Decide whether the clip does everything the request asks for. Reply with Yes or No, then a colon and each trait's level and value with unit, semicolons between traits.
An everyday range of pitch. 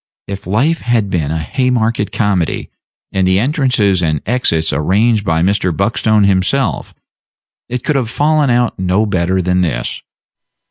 Yes: average, 4.9 semitones